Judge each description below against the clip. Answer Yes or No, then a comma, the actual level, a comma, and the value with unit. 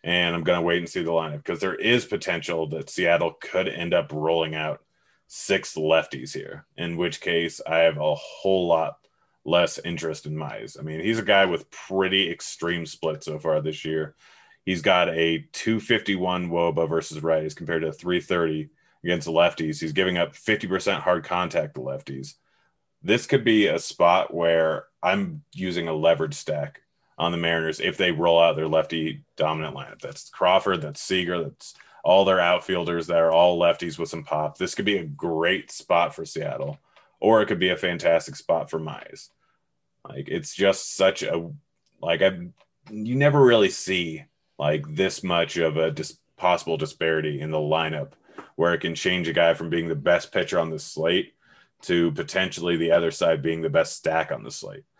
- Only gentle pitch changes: Yes, narrow, 1.8 semitones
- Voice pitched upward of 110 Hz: No, very low, 85 Hz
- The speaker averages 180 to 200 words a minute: Yes, average, 185 wpm